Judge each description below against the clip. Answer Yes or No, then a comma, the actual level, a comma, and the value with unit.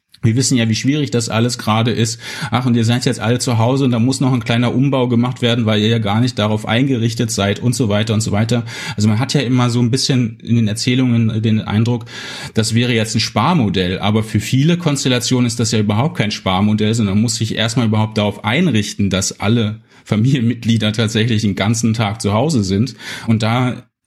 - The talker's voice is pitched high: No, low, 115 Hz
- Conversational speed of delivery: No, fast, 220 wpm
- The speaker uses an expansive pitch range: No, narrow, 2.4 semitones